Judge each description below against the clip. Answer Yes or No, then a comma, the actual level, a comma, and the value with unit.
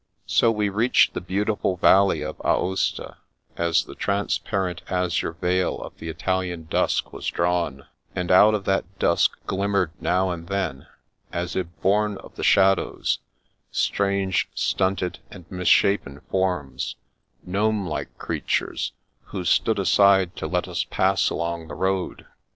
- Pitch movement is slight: Yes, narrow, 2.2 semitones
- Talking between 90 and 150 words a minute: Yes, average, 140 wpm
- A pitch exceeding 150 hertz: No, very low, 95 Hz